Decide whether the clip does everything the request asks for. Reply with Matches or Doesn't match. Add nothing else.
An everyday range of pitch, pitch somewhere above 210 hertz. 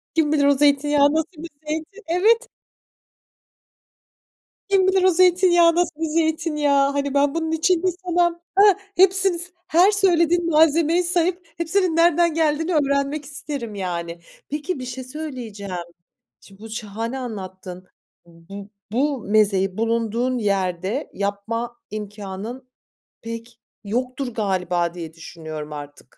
Doesn't match